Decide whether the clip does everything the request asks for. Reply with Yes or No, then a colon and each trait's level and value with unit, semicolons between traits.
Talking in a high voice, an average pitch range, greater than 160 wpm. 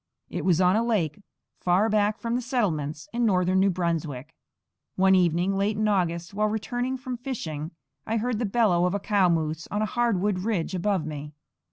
Yes: high, 195 Hz; average, 4.2 semitones; average, 190 wpm